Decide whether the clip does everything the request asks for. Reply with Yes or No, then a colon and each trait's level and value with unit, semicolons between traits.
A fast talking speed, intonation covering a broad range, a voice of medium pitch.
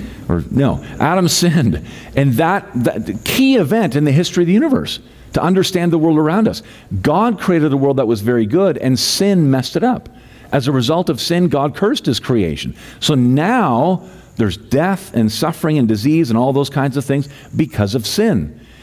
No: average, 195 wpm; wide, 6.0 semitones; medium, 145 Hz